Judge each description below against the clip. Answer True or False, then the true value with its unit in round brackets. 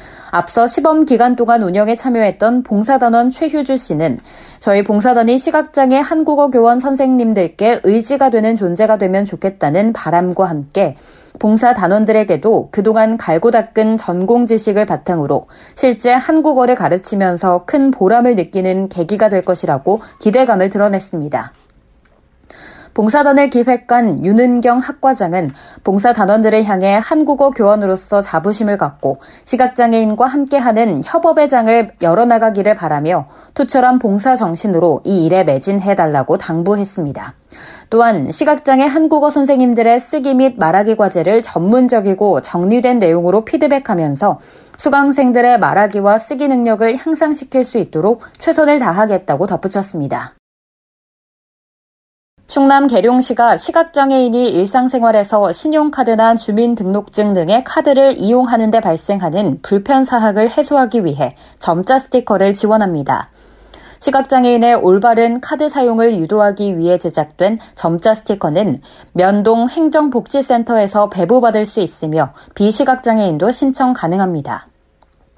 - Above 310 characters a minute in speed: True (325 characters per minute)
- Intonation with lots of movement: False (4.9 semitones)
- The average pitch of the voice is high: True (220 Hz)